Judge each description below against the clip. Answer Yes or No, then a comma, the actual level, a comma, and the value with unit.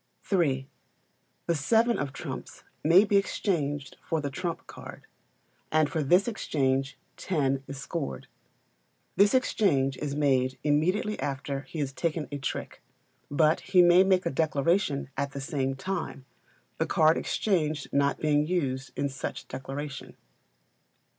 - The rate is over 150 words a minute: No, average, 140 wpm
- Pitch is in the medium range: Yes, medium, 150 Hz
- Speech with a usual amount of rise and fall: Yes, average, 4.2 semitones